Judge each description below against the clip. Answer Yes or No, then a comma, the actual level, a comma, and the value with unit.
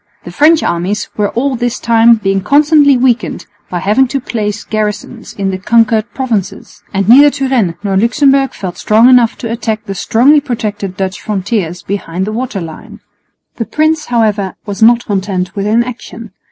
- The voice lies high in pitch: Yes, high, 220 Hz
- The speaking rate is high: No, average, 165 wpm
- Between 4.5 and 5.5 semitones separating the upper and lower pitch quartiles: No, average, 4.1 semitones